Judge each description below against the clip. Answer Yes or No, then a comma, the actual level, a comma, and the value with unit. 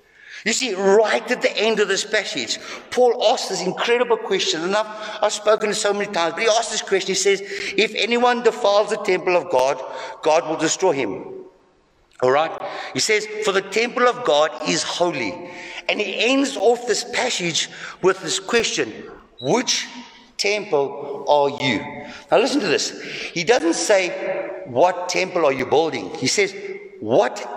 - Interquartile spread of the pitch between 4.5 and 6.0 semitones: Yes, average, 5.3 semitones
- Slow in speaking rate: No, average, 170 wpm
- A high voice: Yes, high, 215 Hz